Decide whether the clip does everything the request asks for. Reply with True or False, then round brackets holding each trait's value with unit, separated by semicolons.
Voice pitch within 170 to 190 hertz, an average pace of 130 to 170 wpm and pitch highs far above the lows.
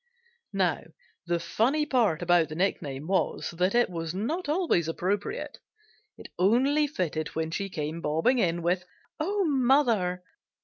True (185 Hz; 140 wpm; 7.5 semitones)